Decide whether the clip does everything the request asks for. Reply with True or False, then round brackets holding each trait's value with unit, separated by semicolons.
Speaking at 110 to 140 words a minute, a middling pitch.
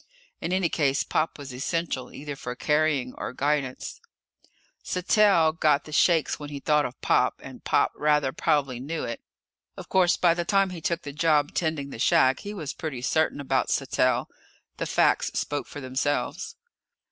False (170 wpm; 150 Hz)